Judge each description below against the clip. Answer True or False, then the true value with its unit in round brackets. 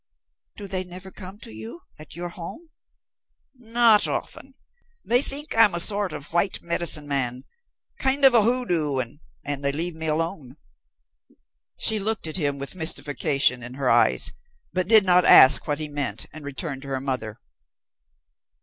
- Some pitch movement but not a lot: False (6.4 semitones)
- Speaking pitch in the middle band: True (165 Hz)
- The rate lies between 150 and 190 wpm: True (160 wpm)